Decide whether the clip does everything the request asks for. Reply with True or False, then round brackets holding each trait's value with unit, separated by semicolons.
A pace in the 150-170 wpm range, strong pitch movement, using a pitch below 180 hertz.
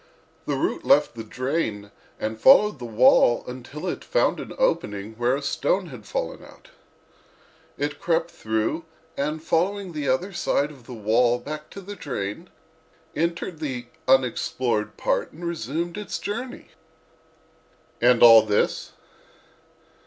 False (140 wpm; 6.4 semitones; 140 Hz)